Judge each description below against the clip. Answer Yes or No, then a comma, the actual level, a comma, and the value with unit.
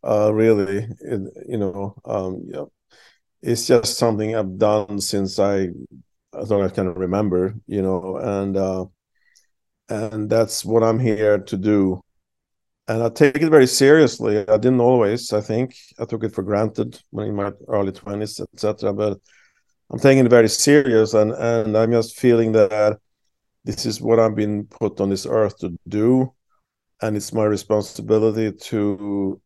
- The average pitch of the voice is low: Yes, low, 105 Hz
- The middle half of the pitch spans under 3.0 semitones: Yes, narrow, 2.4 semitones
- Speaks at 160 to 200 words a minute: Yes, average, 165 wpm